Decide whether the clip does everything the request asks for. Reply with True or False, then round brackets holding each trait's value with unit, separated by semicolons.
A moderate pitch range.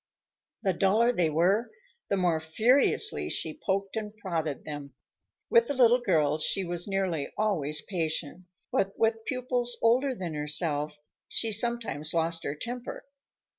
False (6.4 semitones)